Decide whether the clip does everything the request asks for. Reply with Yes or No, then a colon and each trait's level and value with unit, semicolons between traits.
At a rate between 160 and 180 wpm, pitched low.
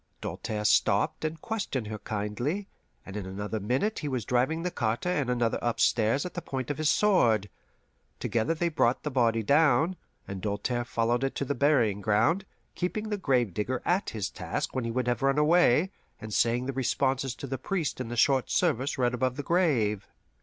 No: average, 190 wpm; low, 130 Hz